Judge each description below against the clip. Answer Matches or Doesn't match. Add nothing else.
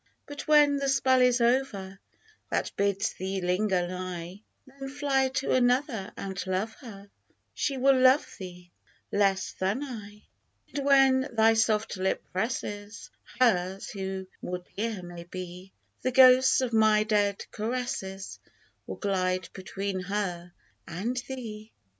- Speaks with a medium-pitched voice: Doesn't match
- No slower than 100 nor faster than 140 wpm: Matches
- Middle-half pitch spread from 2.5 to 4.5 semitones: Doesn't match